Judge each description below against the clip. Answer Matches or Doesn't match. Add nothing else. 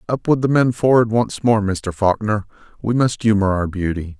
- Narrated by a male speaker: Matches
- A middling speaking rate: Matches